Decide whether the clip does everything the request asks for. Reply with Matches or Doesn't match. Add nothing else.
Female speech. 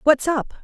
Matches